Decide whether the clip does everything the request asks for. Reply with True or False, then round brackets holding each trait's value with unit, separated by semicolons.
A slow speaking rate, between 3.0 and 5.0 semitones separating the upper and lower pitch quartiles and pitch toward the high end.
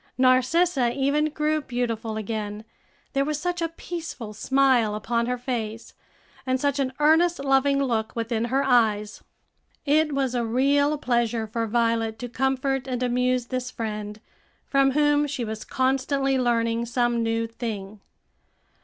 False (145 wpm; 3.3 semitones; 250 Hz)